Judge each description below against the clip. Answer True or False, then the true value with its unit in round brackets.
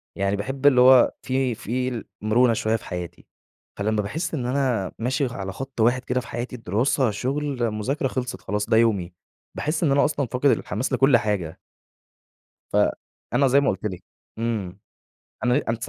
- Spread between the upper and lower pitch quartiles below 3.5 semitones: False (3.8 semitones)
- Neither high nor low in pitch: False (120 Hz)